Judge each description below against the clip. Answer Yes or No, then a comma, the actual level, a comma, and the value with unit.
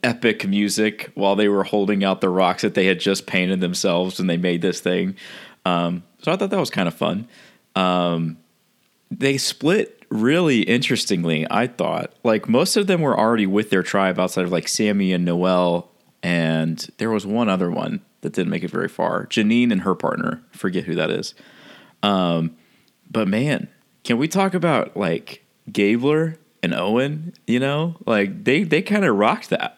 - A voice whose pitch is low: Yes, low, 100 Hz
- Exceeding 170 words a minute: Yes, average, 185 wpm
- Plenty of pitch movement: Yes, wide, 7.1 semitones